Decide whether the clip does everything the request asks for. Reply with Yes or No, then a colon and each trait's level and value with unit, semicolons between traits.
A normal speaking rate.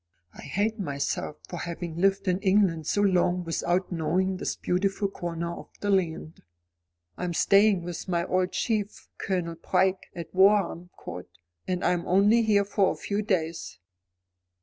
Yes: average, 155 wpm